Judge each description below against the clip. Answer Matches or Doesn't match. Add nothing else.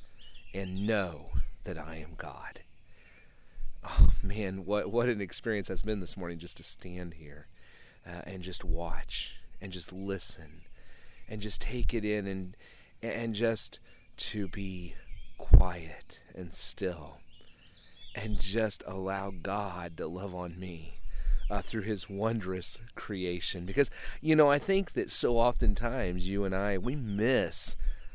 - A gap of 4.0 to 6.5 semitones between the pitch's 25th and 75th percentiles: Doesn't match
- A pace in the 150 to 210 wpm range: Doesn't match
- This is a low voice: Matches